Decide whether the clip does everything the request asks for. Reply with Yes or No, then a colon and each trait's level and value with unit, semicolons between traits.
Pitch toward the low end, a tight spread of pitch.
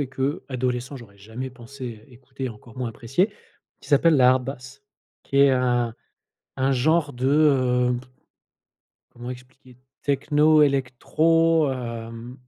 Yes: low, 130 Hz; narrow, 2.2 semitones